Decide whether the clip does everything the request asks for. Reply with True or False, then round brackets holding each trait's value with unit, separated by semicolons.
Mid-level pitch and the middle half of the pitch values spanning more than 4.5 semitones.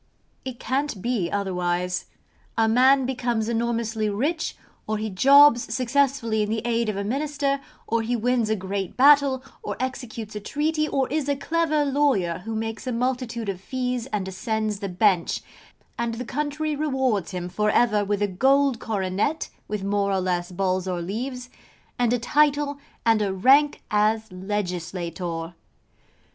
False (225 Hz; 5.0 semitones)